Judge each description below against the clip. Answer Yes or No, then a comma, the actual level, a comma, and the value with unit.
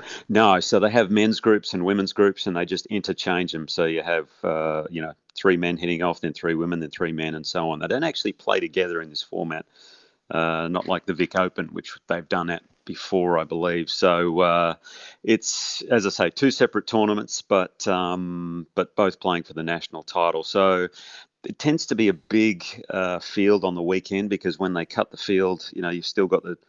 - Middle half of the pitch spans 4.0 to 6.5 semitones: No, average, 2.8 semitones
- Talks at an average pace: No, fast, 215 wpm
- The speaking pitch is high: No, very low, 90 Hz